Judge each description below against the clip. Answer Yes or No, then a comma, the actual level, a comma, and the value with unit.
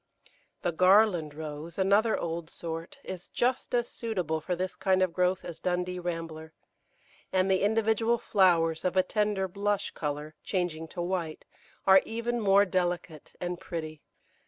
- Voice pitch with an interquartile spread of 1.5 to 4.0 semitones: Yes, average, 3.3 semitones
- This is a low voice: No, medium, 180 Hz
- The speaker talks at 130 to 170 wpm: Yes, average, 150 wpm